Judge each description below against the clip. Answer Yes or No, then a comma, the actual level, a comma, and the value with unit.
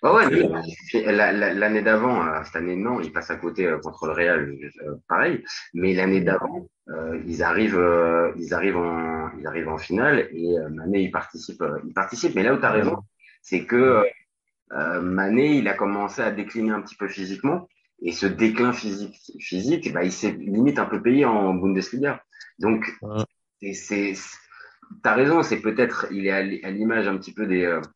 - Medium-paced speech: Yes, average, 170 wpm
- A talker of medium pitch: No, very low, 95 Hz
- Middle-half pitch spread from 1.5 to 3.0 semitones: No, average, 3.6 semitones